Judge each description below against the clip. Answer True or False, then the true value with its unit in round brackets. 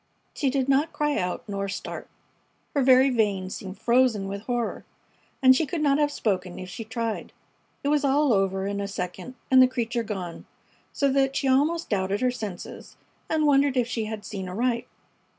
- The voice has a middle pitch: False (240 Hz)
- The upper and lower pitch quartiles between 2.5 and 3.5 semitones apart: False (5.5 semitones)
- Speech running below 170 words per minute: False (185 wpm)